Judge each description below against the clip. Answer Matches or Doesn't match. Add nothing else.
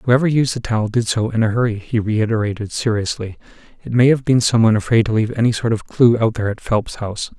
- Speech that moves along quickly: Matches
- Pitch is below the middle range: Matches